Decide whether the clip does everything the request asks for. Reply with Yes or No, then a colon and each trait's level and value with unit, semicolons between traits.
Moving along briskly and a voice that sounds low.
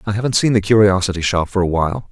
Yes: fast, 255 wpm; low, 100 Hz